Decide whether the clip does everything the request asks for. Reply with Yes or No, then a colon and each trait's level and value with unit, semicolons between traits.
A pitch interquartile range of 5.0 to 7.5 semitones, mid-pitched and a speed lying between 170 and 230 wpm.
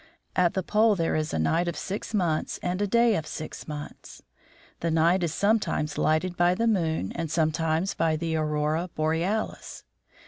No: average, 3.2 semitones; medium, 165 Hz; average, 175 wpm